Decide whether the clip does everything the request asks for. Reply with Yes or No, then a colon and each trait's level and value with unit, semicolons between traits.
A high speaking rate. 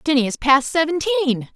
No: average, 155 wpm